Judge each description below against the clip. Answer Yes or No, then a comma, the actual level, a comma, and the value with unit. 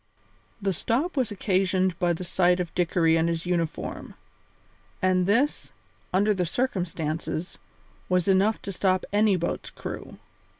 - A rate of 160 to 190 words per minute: No, slow, 135 wpm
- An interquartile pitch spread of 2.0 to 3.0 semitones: Yes, narrow, 2.6 semitones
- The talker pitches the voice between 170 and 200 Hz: Yes, medium, 185 Hz